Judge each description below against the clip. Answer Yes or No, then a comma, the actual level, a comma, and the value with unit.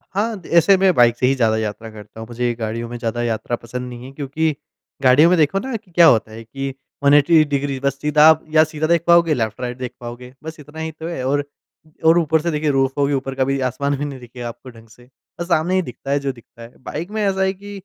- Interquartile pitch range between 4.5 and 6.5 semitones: Yes, average, 4.8 semitones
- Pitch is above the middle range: No, medium, 140 Hz